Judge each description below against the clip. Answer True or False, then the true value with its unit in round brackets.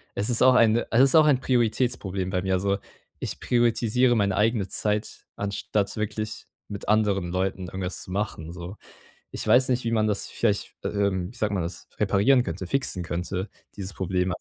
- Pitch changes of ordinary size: True (3.6 semitones)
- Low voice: True (105 Hz)